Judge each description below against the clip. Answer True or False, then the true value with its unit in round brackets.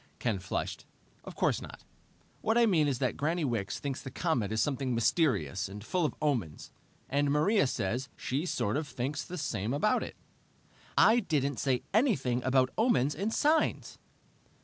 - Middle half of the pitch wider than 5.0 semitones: True (5.4 semitones)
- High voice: False (140 Hz)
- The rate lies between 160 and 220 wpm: True (170 wpm)